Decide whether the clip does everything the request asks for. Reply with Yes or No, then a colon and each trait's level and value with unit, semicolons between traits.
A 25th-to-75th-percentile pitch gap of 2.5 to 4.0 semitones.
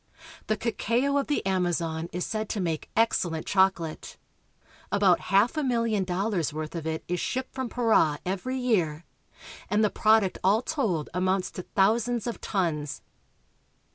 No: average, 4.9 semitones